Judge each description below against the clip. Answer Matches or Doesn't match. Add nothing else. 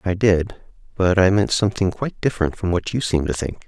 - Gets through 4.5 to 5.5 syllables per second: Doesn't match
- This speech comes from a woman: Doesn't match